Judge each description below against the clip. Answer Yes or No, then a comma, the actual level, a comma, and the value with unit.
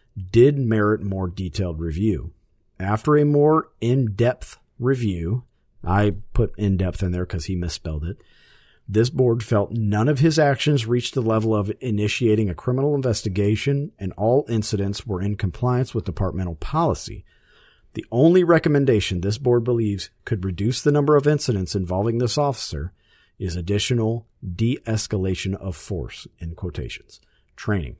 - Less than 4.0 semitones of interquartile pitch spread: No, average, 4.6 semitones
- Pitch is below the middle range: Yes, low, 110 Hz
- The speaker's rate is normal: Yes, average, 150 wpm